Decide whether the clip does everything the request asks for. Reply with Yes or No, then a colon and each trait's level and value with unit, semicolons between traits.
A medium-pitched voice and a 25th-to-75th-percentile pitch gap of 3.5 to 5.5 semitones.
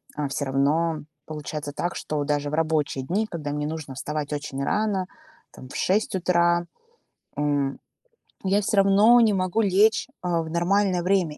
Yes: medium, 165 Hz; average, 4.7 semitones